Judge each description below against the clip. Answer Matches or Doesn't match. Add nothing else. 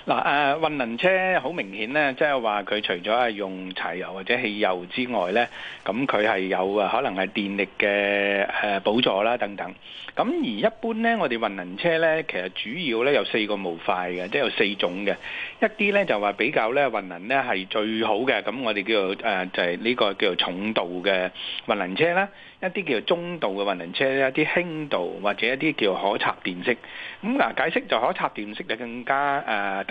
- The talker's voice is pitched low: Matches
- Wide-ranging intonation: Matches